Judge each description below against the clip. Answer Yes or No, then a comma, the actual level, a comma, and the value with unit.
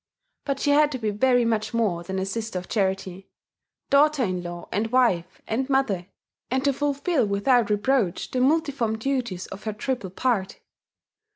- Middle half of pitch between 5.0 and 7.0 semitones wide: Yes, wide, 5.6 semitones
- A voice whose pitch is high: Yes, high, 230 Hz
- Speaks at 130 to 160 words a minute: No, average, 170 wpm